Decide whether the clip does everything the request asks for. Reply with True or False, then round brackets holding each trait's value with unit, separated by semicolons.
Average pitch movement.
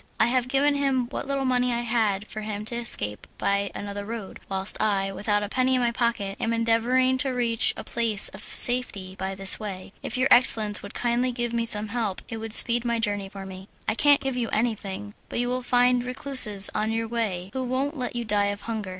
True (3.4 semitones)